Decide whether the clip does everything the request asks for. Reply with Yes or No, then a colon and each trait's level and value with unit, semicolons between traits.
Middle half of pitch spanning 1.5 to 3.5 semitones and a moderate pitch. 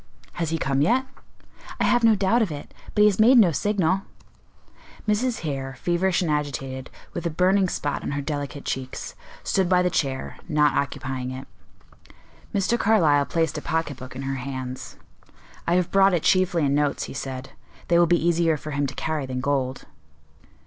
No: average, 5.2 semitones; medium, 160 Hz